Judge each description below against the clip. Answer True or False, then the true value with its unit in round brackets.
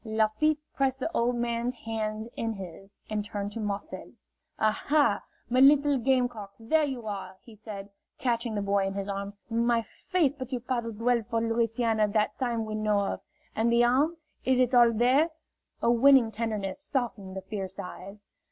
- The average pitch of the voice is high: True (230 Hz)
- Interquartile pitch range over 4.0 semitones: False (3.1 semitones)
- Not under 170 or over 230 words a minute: True (180 wpm)